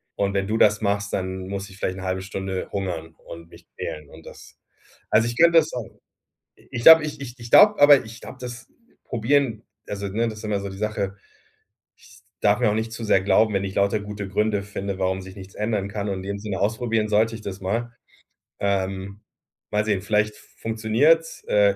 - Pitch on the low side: Yes, low, 105 Hz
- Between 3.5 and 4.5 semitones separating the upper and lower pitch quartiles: No, narrow, 2.6 semitones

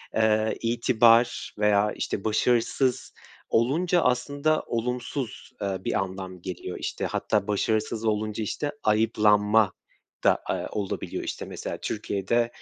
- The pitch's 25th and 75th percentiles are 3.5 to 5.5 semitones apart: No, narrow, 2.6 semitones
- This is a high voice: No, low, 110 Hz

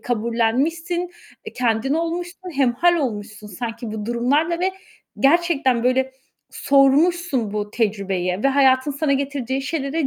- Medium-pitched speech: No, very high, 270 Hz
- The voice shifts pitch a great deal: Yes, wide, 5.8 semitones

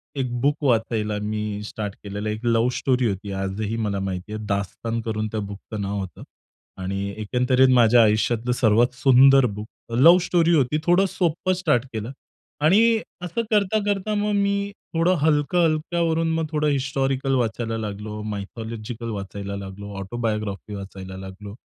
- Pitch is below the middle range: Yes, low, 115 Hz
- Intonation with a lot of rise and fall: Yes, wide, 5.7 semitones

